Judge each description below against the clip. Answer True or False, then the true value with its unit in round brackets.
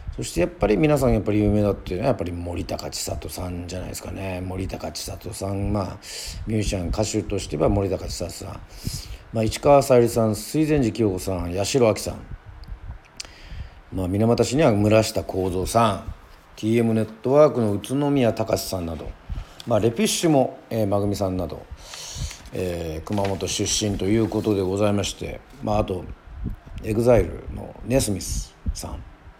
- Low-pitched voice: True (100 Hz)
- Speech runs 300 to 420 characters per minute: True (345 characters per minute)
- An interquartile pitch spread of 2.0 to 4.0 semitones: True (3.6 semitones)